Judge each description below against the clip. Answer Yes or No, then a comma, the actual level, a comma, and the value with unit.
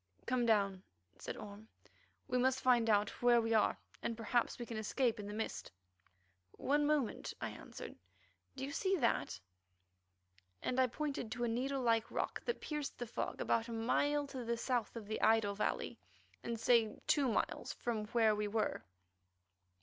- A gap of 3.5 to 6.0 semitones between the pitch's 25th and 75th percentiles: No, average, 2.9 semitones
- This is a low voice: No, high, 235 Hz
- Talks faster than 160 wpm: Yes, average, 170 wpm